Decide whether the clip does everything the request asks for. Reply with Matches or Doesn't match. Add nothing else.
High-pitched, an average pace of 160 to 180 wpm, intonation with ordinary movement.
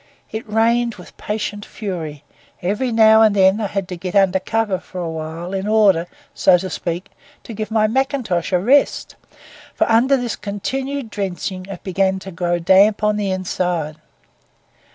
Matches